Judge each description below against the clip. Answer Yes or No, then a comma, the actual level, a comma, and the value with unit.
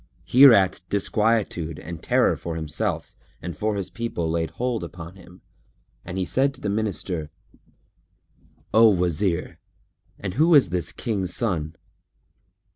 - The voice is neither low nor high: No, very low, 95 Hz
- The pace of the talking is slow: Yes, slow, 130 wpm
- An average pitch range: Yes, average, 4.7 semitones